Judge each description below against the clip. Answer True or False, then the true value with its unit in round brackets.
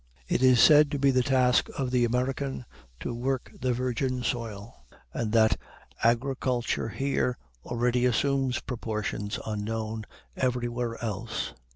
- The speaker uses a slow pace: True (130 wpm)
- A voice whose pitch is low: True (125 Hz)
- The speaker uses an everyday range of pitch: False (2.1 semitones)